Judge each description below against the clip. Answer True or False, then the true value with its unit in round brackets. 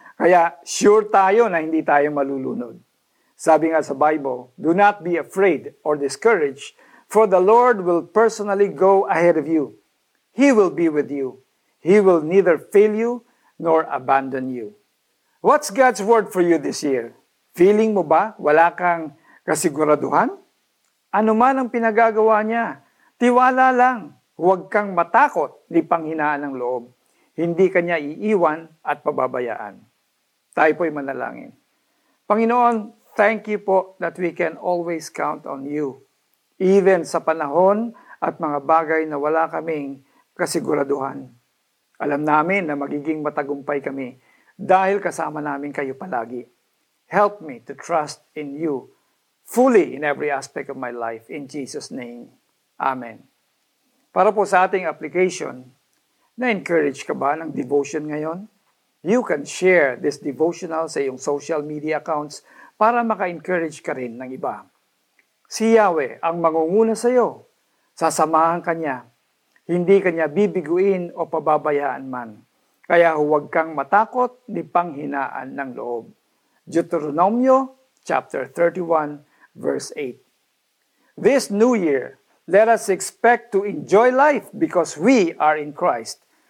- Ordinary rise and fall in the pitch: False (5.9 semitones)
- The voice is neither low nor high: True (170 Hz)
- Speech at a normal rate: True (135 wpm)